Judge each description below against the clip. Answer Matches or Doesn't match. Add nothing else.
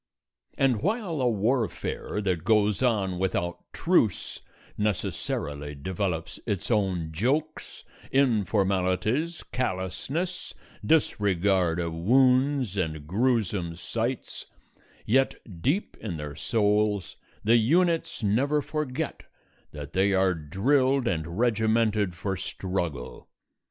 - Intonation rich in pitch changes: Matches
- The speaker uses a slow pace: Matches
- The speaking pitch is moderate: Doesn't match